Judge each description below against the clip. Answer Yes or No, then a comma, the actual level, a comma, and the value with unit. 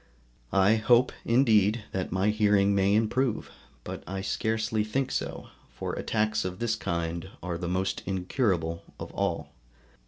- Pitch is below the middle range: Yes, low, 105 Hz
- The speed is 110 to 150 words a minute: Yes, average, 145 wpm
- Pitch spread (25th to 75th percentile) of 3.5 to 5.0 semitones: No, average, 3.1 semitones